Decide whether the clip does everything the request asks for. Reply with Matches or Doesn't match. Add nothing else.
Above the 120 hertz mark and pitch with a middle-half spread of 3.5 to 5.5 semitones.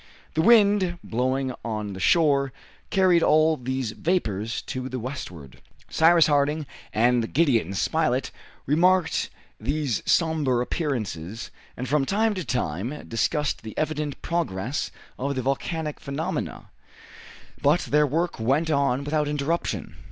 Matches